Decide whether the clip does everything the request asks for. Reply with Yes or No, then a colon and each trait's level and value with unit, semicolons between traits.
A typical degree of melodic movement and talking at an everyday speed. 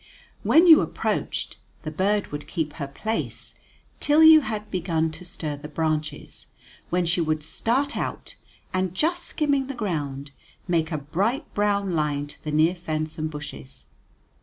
No: wide, 5.8 semitones; average, 160 wpm